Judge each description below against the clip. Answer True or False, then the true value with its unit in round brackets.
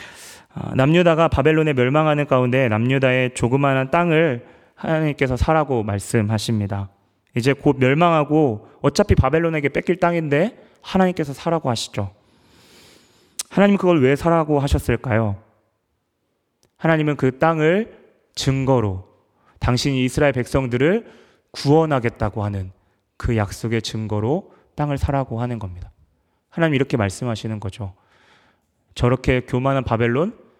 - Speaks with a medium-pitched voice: False (130 Hz)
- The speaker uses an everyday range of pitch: False (5.7 semitones)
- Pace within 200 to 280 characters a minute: False (300 characters per minute)